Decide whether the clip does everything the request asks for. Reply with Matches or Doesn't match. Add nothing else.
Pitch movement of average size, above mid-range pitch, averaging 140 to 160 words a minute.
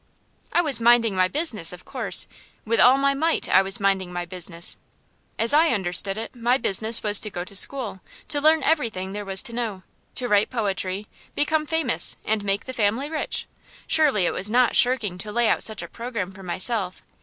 Doesn't match